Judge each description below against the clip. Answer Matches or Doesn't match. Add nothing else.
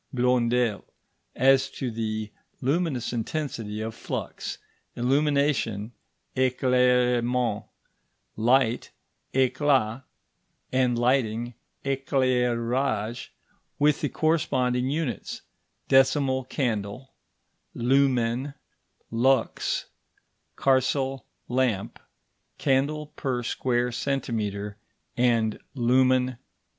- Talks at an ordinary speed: Doesn't match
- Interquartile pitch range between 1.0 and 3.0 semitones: Matches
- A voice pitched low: Matches